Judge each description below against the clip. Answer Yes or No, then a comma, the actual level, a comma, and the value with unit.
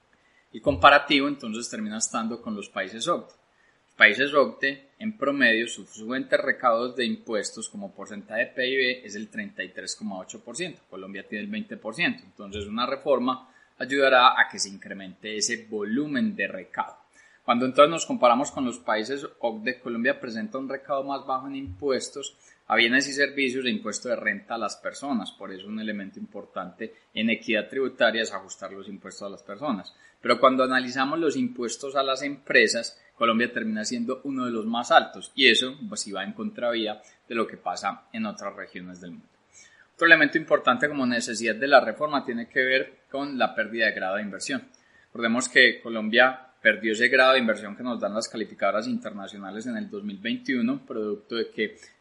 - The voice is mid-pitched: No, low, 130 Hz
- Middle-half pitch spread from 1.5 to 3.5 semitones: No, average, 4.6 semitones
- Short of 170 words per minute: No, average, 175 wpm